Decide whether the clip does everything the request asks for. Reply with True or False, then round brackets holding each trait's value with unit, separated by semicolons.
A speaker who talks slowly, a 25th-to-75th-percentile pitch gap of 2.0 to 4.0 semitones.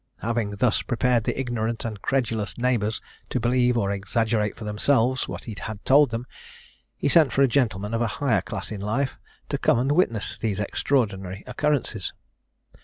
False (175 wpm; 3.4 semitones)